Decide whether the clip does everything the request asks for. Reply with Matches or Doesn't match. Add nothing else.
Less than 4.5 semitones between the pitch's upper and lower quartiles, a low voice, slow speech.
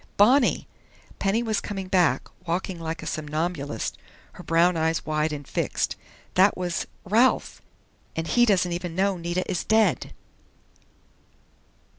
Doesn't match